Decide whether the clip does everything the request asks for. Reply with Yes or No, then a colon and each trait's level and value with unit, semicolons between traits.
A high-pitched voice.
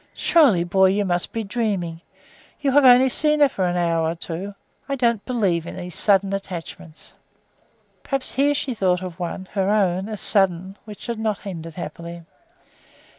Yes: high, 195 Hz